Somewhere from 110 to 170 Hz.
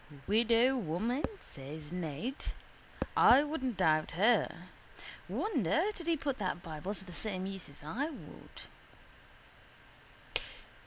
No: high, 205 Hz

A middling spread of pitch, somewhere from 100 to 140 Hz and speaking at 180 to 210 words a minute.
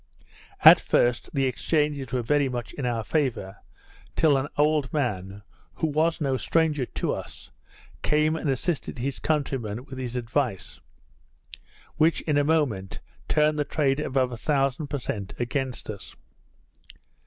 No: average, 3.7 semitones; low, 135 Hz; average, 145 wpm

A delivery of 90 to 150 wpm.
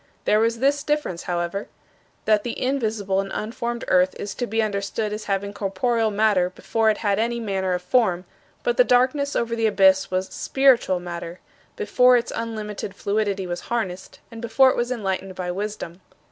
No: average, 175 wpm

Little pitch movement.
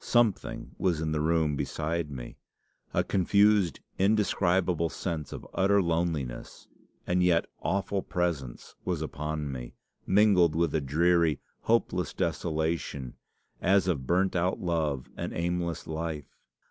No: average, 3.1 semitones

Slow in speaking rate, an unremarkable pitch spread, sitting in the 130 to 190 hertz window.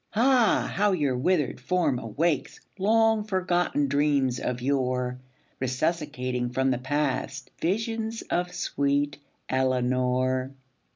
No: slow, 105 wpm; wide, 5.8 semitones; medium, 140 Hz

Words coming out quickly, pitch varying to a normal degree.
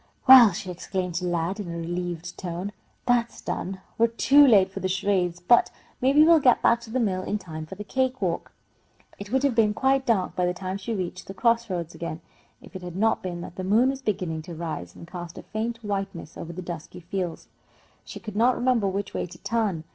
Yes: fast, 225 wpm; average, 4.7 semitones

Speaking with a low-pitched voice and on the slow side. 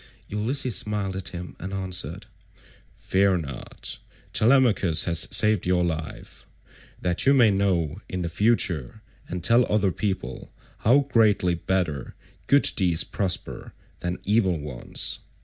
Yes: very low, 95 Hz; slow, 125 wpm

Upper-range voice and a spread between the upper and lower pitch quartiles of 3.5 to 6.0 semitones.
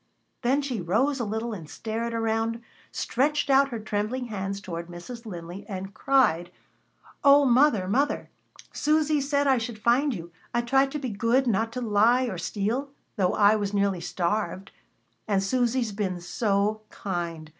Yes: high, 225 Hz; average, 4.7 semitones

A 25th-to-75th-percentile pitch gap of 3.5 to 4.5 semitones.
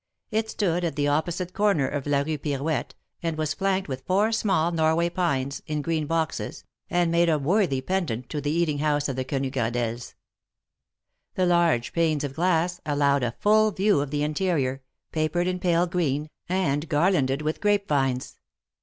Yes: average, 4.0 semitones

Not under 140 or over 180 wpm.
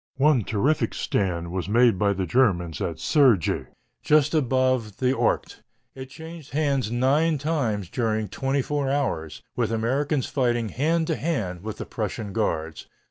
Yes: average, 150 wpm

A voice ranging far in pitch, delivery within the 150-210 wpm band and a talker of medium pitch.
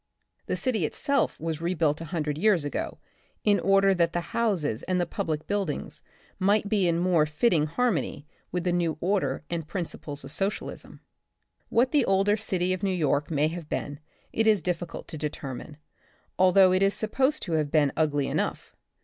No: average, 4.4 semitones; average, 180 wpm; medium, 175 Hz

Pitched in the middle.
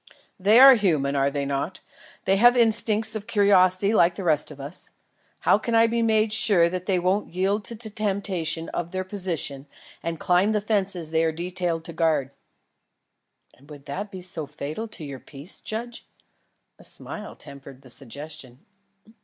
Yes: medium, 180 Hz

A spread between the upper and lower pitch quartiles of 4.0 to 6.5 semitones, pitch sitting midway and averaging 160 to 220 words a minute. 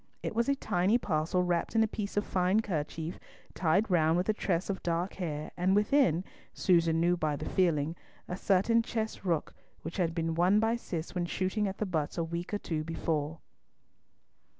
No: average, 3.6 semitones; medium, 180 Hz; average, 195 wpm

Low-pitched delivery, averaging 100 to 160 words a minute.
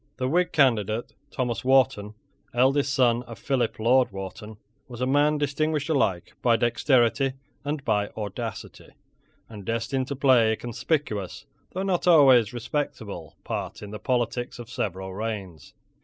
Yes: low, 120 Hz; average, 145 wpm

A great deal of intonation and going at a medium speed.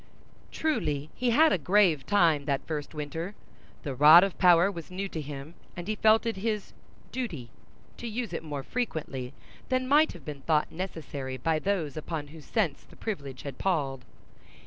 Yes: wide, 5.8 semitones; average, 175 wpm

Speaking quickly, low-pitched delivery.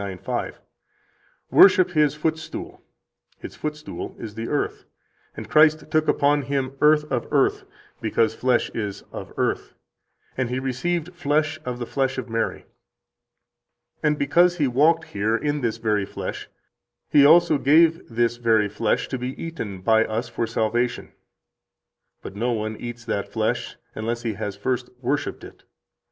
No: average, 155 wpm; low, 130 Hz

